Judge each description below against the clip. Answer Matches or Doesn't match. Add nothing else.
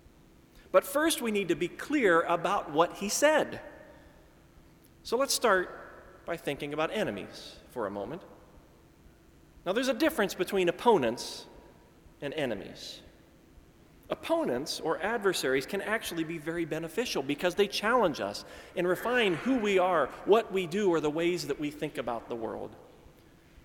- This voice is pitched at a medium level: Matches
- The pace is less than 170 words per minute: Matches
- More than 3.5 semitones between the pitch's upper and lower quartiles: Matches